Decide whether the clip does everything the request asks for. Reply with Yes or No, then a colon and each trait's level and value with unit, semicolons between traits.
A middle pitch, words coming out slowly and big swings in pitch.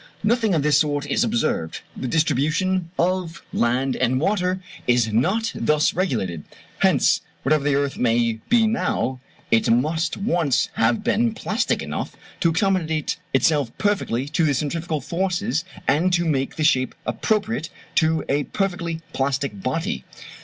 No: medium, 160 Hz; average, 145 wpm; wide, 5.8 semitones